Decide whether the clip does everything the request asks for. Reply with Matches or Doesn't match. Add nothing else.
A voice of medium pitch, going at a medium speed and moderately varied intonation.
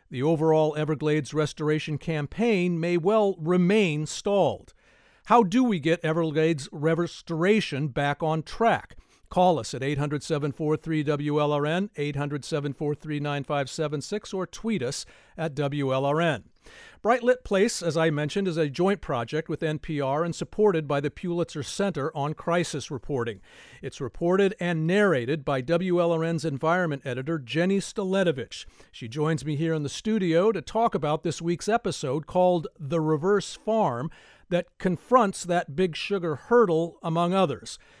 Doesn't match